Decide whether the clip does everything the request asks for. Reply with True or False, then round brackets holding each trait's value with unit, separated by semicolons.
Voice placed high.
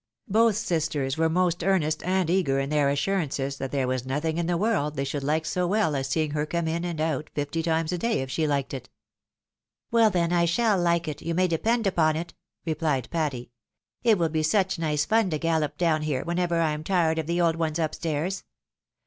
False (160 Hz)